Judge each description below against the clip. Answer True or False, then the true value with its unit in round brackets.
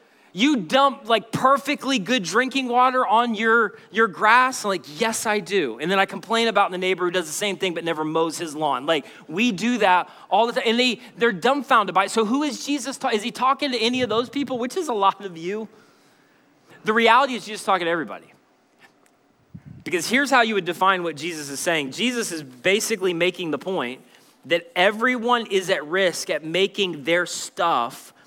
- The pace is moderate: False (210 wpm)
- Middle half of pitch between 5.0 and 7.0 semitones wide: True (5.5 semitones)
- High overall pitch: True (210 Hz)